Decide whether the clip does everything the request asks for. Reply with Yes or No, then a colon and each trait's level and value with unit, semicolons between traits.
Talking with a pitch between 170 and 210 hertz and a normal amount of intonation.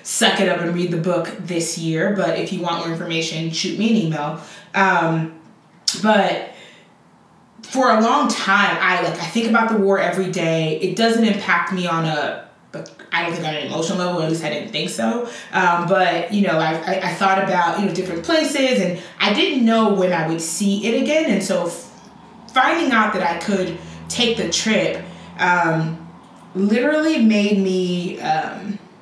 Yes: medium, 185 Hz; average, 4.0 semitones